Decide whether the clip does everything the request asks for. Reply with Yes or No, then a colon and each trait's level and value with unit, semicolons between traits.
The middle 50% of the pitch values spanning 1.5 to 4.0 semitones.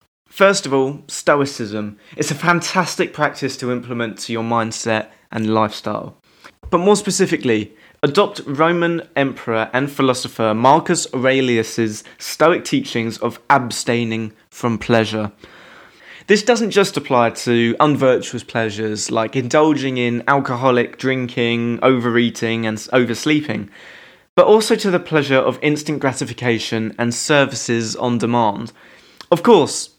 No: average, 4.6 semitones